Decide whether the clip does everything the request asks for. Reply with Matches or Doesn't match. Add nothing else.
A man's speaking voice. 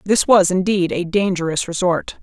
Doesn't match